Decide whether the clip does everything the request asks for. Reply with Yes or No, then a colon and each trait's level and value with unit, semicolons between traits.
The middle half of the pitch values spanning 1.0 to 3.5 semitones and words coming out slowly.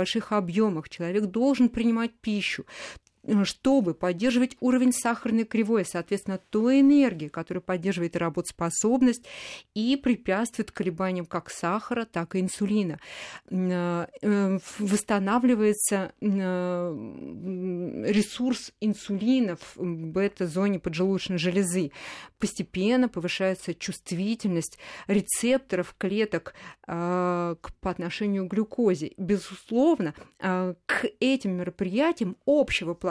No: average, 4.0 semitones; slow, 85 wpm